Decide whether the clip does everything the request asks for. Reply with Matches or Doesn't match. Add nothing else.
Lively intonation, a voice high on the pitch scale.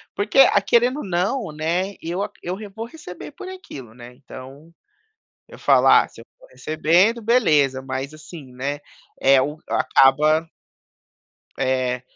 Doesn't match